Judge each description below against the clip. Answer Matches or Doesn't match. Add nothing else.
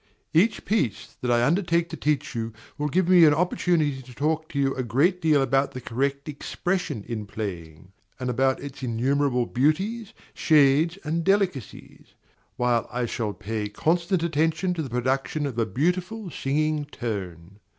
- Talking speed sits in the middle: Matches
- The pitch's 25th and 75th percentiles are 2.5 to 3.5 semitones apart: Doesn't match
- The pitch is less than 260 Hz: Matches